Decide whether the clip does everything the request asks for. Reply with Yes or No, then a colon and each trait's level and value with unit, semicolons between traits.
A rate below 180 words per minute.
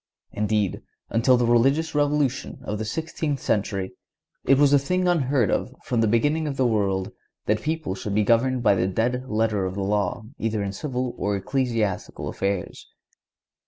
Yes: average, 170 wpm